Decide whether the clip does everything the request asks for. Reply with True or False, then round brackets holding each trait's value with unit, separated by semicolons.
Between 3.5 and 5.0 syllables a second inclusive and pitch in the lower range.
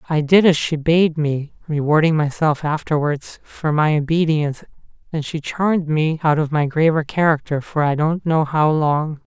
False (4.7 syllables/s; 155 Hz)